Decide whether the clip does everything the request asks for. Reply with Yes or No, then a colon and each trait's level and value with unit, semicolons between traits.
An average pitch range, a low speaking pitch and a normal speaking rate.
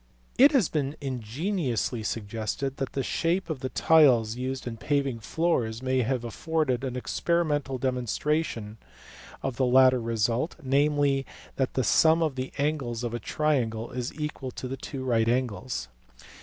Yes: average, 3.8 semitones; low, 130 Hz; average, 150 wpm